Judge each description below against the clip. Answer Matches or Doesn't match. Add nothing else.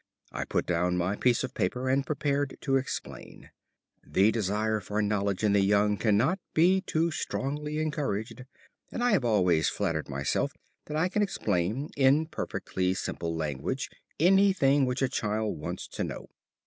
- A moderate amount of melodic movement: Doesn't match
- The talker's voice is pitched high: Doesn't match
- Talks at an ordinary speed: Matches